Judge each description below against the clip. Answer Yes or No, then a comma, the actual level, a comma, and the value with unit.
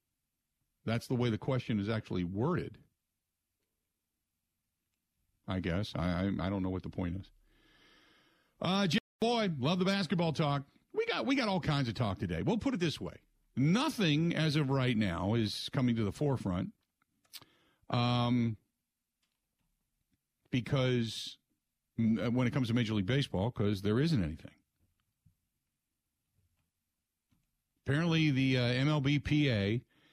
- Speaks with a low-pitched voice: Yes, low, 115 Hz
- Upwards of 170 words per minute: No, slow, 135 wpm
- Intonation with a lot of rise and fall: Yes, wide, 7.7 semitones